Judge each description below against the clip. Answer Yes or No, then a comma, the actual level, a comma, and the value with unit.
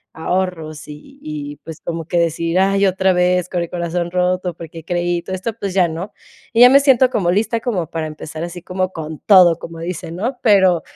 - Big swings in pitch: No, narrow, 2.5 semitones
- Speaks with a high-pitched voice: No, medium, 180 Hz